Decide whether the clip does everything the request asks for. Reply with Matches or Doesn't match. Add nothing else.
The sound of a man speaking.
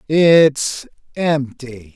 Matches